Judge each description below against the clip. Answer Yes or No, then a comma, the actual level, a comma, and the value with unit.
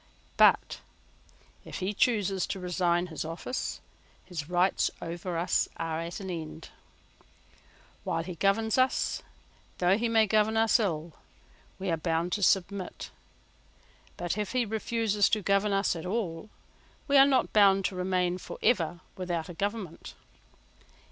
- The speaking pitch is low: No, high, 190 Hz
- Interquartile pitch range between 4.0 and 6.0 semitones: No, average, 3.5 semitones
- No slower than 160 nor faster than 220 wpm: No, average, 145 wpm